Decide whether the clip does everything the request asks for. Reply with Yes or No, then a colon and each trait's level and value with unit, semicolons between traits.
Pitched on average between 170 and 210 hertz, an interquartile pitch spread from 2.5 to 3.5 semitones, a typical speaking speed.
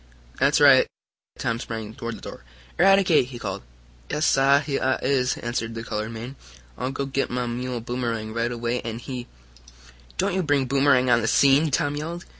No: low, 125 Hz; average, 3.1 semitones; average, 190 wpm